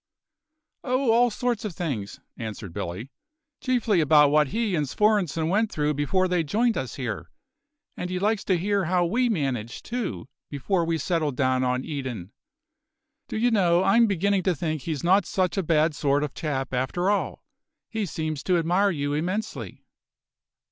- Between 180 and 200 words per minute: No, average, 170 wpm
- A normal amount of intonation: No, wide, 6.0 semitones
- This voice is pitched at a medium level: Yes, medium, 170 Hz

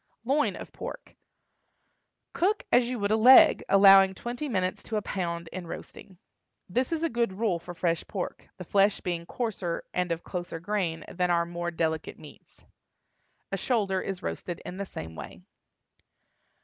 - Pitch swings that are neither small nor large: Yes, average, 4.2 semitones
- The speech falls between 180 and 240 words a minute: No, average, 165 wpm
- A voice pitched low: No, high, 190 Hz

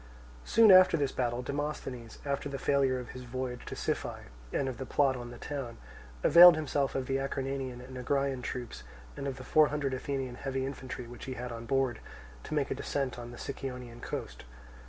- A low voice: Yes, low, 130 Hz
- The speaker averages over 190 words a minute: Yes, average, 200 wpm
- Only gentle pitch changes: Yes, narrow, 2.0 semitones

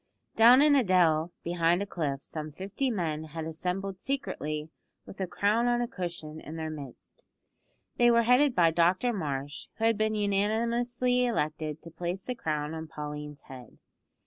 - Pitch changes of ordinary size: No, wide, 6.8 semitones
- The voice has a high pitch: No, medium, 180 Hz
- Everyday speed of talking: Yes, average, 170 wpm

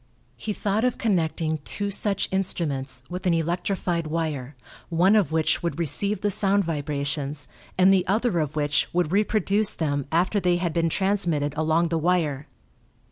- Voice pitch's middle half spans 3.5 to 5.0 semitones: Yes, average, 4.1 semitones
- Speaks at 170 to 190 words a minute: No, average, 160 wpm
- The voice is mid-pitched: Yes, medium, 170 Hz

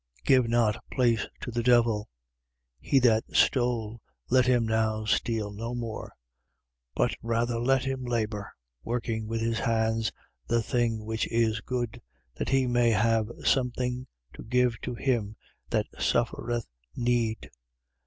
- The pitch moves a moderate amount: No, narrow, 1.7 semitones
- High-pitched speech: No, low, 115 Hz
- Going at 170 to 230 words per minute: No, average, 145 wpm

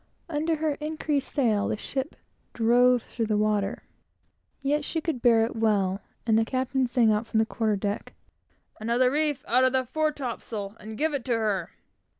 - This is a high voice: Yes, high, 240 Hz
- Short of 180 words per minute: No, average, 185 wpm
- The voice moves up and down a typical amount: Yes, average, 4.3 semitones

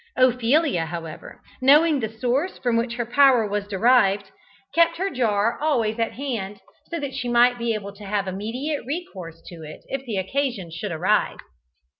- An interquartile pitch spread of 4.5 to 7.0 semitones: Yes, average, 5.1 semitones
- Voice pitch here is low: No, high, 235 Hz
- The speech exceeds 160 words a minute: Yes, average, 170 wpm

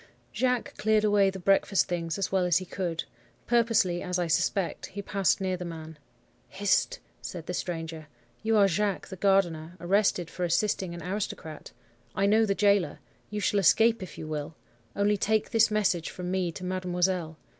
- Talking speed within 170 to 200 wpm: Yes, average, 175 wpm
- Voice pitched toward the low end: No, medium, 185 Hz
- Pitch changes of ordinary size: Yes, average, 3.0 semitones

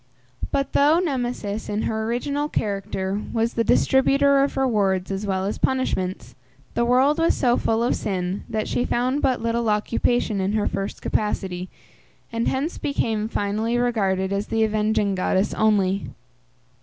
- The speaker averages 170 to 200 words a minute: No, average, 155 wpm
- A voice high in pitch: Yes, high, 220 Hz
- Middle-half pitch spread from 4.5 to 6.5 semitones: No, average, 3.9 semitones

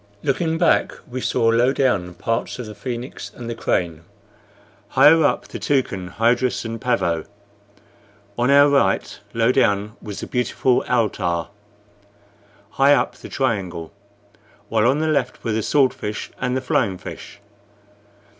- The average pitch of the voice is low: Yes, low, 120 Hz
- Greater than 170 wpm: No, average, 145 wpm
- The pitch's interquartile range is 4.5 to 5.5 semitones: No, average, 4.1 semitones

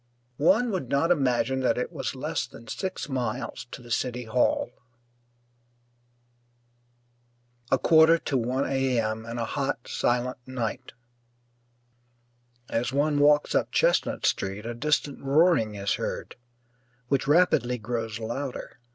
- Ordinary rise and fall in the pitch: Yes, average, 3.4 semitones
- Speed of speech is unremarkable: No, slow, 130 wpm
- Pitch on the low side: Yes, low, 130 Hz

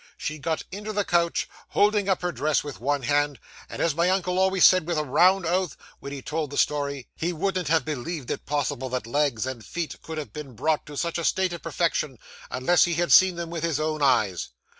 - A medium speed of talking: No, fast, 225 wpm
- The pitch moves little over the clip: No, average, 3.6 semitones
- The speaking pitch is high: No, medium, 155 Hz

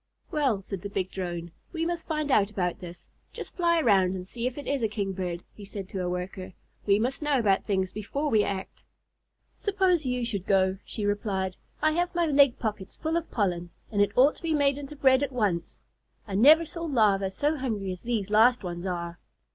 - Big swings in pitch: Yes, wide, 7.0 semitones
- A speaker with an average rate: No, fast, 210 wpm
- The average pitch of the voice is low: No, high, 215 Hz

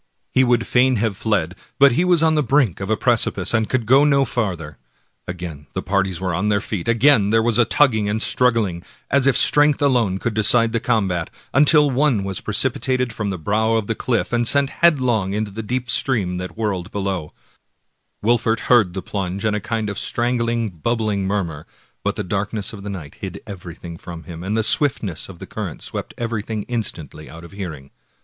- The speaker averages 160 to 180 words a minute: No, average, 200 wpm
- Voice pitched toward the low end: Yes, low, 110 Hz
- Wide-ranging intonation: No, average, 4.2 semitones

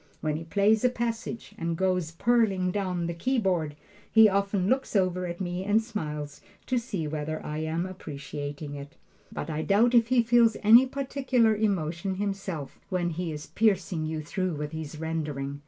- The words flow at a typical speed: Yes, average, 170 wpm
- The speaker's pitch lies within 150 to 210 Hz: Yes, medium, 185 Hz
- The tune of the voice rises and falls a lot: Yes, wide, 5.7 semitones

